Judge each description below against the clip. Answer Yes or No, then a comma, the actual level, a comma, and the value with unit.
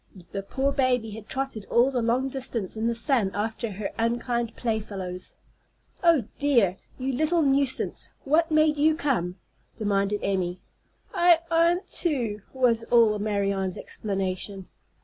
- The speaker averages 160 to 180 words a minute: No, slow, 135 wpm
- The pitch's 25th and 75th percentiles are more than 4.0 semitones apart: Yes, average, 5.1 semitones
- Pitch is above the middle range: Yes, high, 235 Hz